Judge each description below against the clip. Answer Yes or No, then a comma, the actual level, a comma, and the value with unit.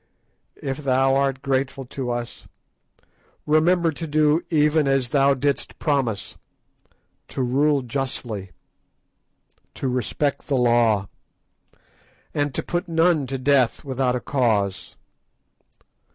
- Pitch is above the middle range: No, low, 135 Hz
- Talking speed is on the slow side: Yes, slow, 110 wpm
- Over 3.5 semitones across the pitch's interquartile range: No, average, 2.8 semitones